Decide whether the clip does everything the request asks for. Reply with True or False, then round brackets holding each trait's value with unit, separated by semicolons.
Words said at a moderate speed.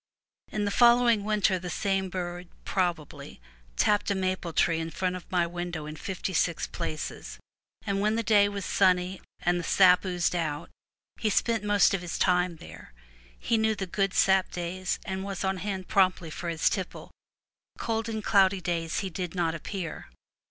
True (180 wpm)